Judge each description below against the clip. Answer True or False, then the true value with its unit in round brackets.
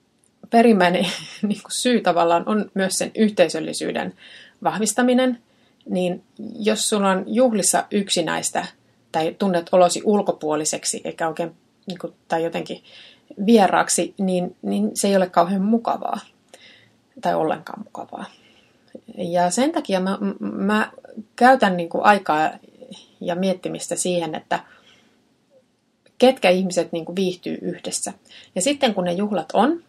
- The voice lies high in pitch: True (195 Hz)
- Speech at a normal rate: True (110 wpm)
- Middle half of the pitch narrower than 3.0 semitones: False (4.7 semitones)